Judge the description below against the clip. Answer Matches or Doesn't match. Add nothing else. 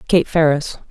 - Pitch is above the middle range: Doesn't match